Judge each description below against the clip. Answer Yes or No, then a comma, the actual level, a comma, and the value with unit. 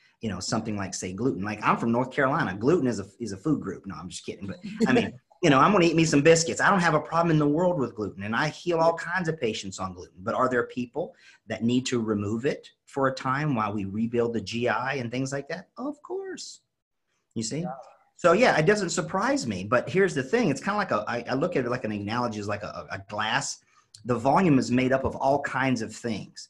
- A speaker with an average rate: No, fast, 265 wpm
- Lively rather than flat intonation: Yes, wide, 6.4 semitones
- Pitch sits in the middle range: No, low, 130 Hz